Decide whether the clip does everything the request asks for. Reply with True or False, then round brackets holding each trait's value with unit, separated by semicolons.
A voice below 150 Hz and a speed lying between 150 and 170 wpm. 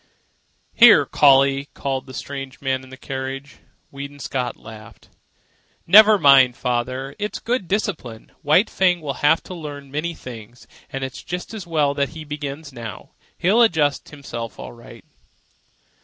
True (140 Hz; 155 wpm)